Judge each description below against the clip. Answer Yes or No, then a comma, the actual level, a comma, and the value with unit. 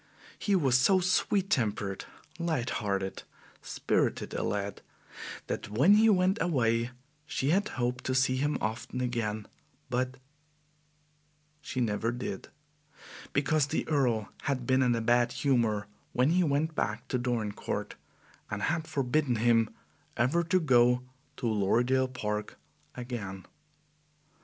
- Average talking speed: No, slow, 130 wpm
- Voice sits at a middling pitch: No, low, 125 Hz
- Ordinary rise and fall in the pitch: Yes, average, 4.3 semitones